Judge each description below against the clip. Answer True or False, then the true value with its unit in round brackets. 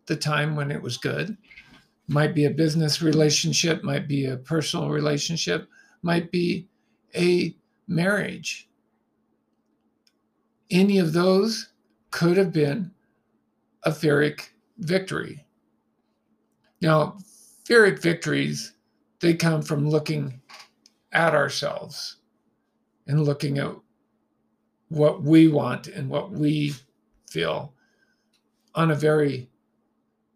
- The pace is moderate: False (100 wpm)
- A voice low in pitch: False (155 Hz)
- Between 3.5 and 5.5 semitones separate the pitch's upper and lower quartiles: False (3.1 semitones)